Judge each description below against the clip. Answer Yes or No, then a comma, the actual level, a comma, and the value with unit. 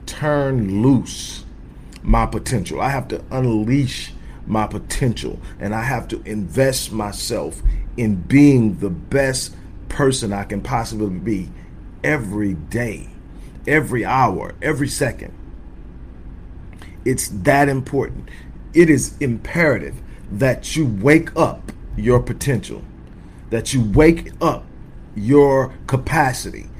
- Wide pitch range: Yes, wide, 6.7 semitones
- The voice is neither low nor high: No, low, 110 Hz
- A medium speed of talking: No, slow, 110 wpm